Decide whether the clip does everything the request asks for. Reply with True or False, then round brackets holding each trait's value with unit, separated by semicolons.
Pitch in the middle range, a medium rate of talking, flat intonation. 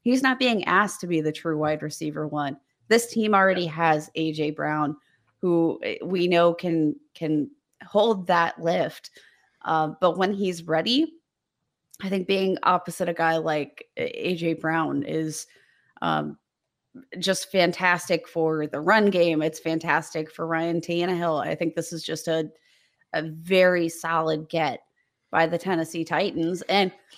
False (170 Hz; 150 wpm; 3.0 semitones)